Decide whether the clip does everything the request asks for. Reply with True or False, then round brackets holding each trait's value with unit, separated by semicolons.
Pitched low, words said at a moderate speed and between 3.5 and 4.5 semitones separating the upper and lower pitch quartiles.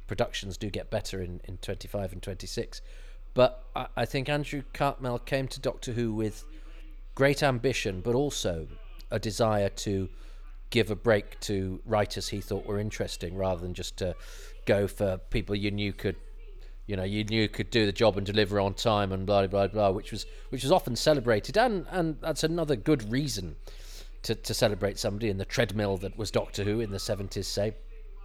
True (105 Hz; 190 wpm; 3.8 semitones)